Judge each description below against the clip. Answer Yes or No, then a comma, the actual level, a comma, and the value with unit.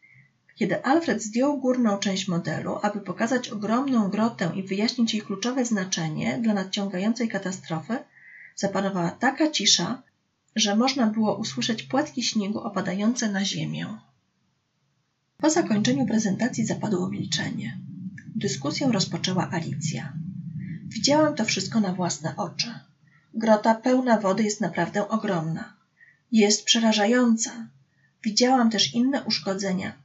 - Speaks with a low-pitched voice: No, high, 210 Hz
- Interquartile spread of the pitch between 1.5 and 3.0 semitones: No, average, 3.8 semitones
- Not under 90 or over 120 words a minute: Yes, slow, 110 wpm